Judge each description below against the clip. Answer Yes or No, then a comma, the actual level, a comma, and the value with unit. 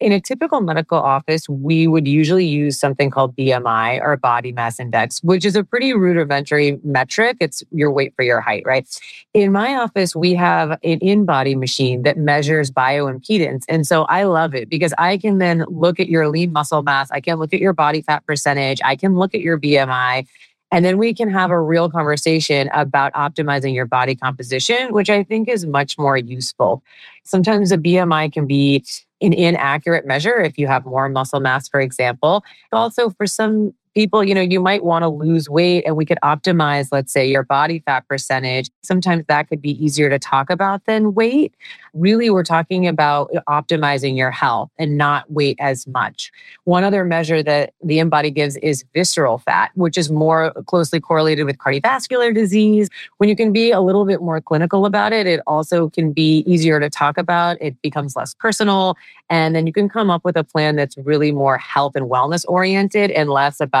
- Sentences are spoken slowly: No, average, 195 wpm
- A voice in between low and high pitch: Yes, medium, 160 Hz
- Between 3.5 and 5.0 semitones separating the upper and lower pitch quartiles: Yes, average, 4.7 semitones